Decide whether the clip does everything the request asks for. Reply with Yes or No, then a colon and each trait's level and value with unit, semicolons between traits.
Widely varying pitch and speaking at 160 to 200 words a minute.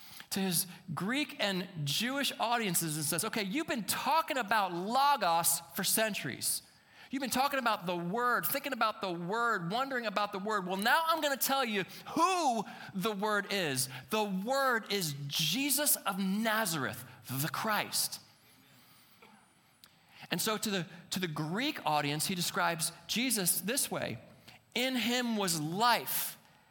No: wide, 6.1 semitones; average, 150 wpm